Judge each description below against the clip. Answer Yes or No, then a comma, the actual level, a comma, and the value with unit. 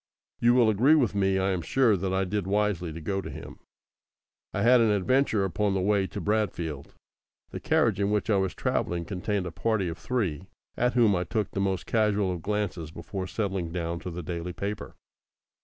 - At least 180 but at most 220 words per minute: Yes, fast, 205 wpm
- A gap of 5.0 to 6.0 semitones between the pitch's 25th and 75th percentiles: No, average, 2.8 semitones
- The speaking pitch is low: Yes, very low, 95 Hz